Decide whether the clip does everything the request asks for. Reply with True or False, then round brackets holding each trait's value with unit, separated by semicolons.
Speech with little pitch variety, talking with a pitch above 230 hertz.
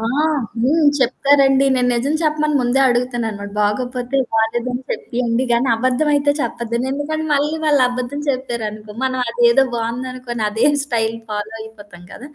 False (3.1 semitones; 245 Hz)